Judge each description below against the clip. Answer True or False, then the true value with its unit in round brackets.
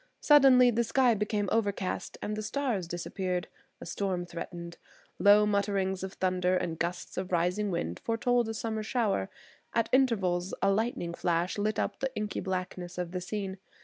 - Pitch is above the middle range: True (195 Hz)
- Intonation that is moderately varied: True (3.5 semitones)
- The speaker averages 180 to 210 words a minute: False (165 wpm)